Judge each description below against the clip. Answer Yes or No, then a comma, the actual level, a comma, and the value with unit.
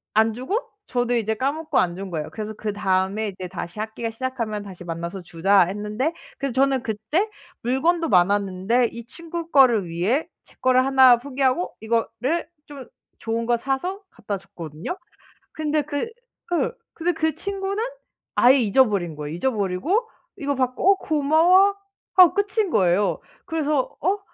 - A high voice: Yes, high, 245 Hz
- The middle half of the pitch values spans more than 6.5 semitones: Yes, wide, 7.3 semitones